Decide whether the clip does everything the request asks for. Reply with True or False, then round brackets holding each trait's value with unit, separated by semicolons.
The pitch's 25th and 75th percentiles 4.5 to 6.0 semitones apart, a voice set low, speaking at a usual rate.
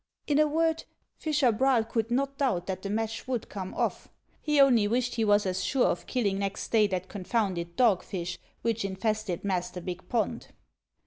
False (4.9 semitones; 220 Hz; 180 wpm)